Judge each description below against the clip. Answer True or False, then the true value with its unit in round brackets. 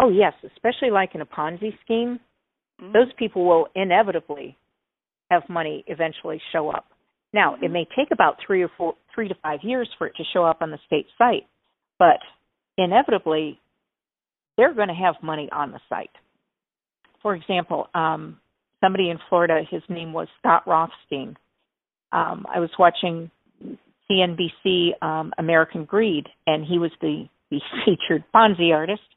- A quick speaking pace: False (155 wpm)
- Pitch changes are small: False (3.6 semitones)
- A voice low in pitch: False (175 Hz)